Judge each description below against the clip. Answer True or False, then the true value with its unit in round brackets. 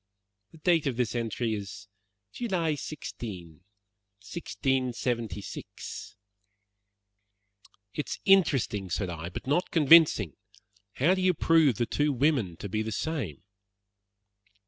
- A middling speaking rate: False (115 wpm)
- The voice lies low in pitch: True (125 Hz)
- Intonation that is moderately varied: False (7.4 semitones)